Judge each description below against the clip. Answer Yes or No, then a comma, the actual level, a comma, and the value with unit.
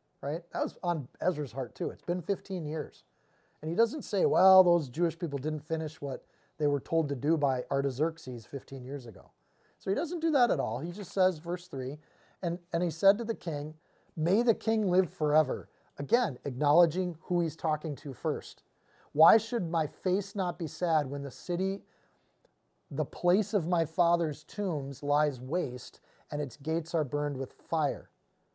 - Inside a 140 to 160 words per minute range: No, average, 185 wpm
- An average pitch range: Yes, average, 4.0 semitones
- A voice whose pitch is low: No, medium, 165 Hz